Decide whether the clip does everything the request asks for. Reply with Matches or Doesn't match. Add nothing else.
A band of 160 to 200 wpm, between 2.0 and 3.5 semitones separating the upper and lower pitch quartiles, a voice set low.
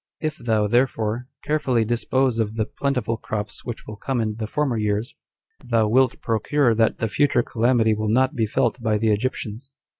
Matches